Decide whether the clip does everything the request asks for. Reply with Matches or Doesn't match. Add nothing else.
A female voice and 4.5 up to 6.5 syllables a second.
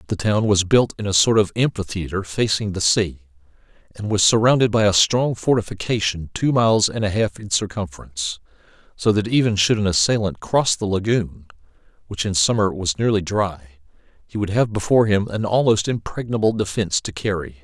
Doesn't match